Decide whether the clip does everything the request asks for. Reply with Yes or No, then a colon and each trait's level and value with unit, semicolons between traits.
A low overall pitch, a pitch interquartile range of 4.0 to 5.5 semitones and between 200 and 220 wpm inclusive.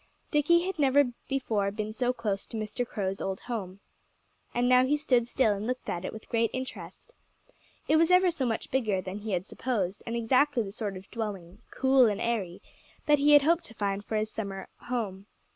No: high, 230 Hz; average, 4.7 semitones; fast, 205 wpm